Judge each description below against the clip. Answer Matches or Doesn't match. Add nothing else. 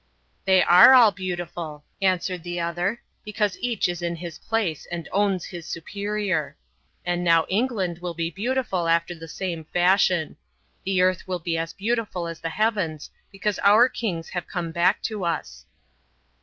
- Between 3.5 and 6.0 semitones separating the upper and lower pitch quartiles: Doesn't match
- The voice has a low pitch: Doesn't match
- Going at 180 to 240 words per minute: Doesn't match